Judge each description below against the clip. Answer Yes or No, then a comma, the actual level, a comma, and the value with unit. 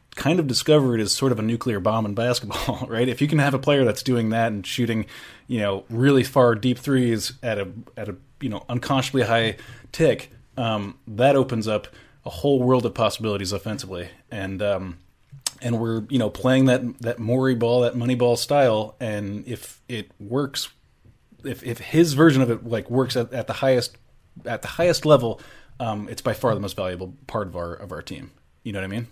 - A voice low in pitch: Yes, low, 120 Hz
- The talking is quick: Yes, fast, 210 wpm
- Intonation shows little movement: No, average, 3.2 semitones